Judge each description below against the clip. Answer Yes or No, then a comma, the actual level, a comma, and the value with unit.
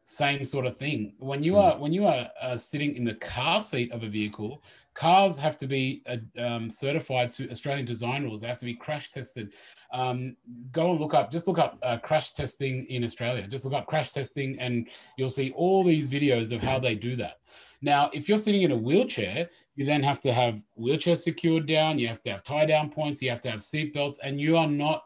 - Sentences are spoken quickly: Yes, fast, 230 wpm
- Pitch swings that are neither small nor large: Yes, average, 3.9 semitones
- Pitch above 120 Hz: Yes, low, 135 Hz